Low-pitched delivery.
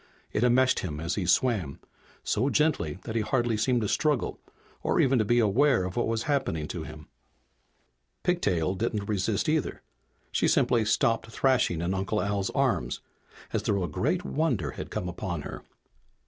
Yes: low, 110 Hz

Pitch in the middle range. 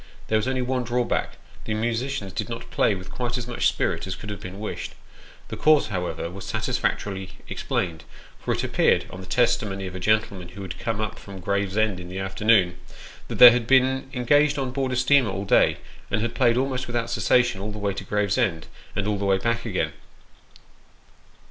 No: low, 110 Hz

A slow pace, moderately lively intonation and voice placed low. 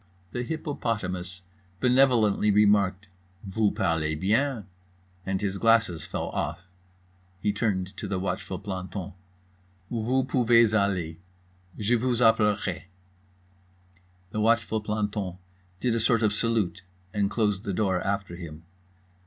Yes: slow, 120 wpm; average, 3.3 semitones; low, 105 Hz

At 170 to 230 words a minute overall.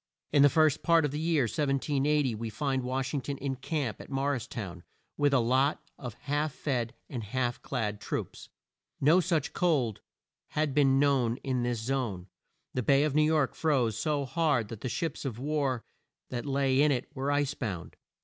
Yes: average, 190 wpm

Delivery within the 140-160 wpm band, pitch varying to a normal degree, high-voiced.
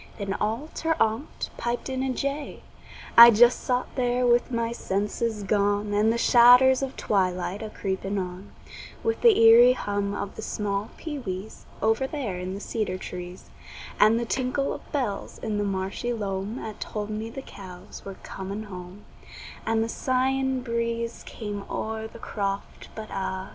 No: average, 170 wpm; average, 3.5 semitones; high, 220 Hz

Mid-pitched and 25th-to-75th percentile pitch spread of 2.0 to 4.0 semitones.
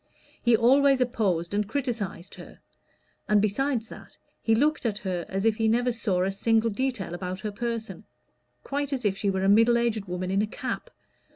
No: high, 220 Hz; average, 3.7 semitones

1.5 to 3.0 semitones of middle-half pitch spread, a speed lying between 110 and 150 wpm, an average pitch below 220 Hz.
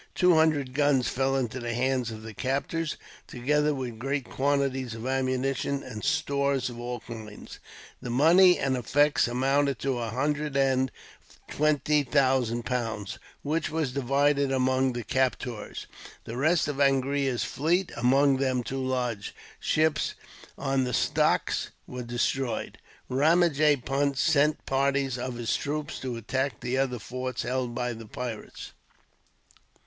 Yes: narrow, 2.5 semitones; average, 140 wpm; low, 135 Hz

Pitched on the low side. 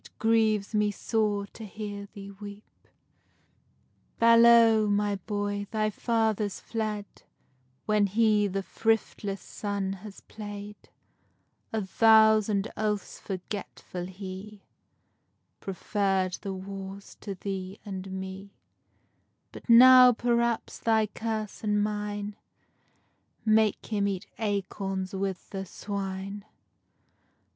No: high, 205 Hz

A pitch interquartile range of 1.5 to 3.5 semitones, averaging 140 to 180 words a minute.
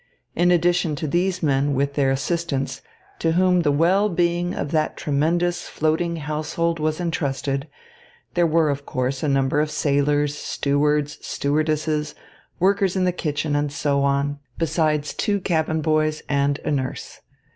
Yes: average, 3.0 semitones; average, 150 wpm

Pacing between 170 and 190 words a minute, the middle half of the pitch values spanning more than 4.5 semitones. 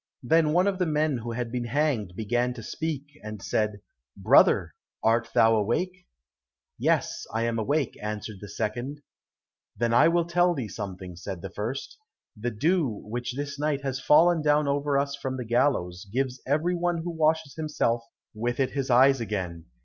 Yes: average, 175 wpm; average, 5.2 semitones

